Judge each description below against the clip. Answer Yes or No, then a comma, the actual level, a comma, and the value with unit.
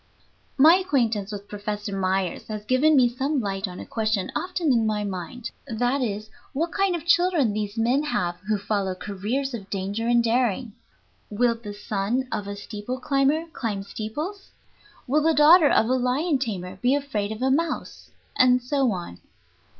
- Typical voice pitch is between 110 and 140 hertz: No, high, 230 Hz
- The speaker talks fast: No, average, 175 wpm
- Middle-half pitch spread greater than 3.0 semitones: Yes, average, 5.1 semitones